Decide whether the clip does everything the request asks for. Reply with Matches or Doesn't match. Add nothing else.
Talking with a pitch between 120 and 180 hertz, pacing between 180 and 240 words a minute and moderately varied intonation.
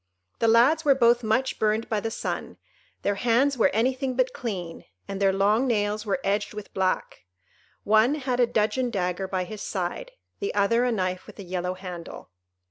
Doesn't match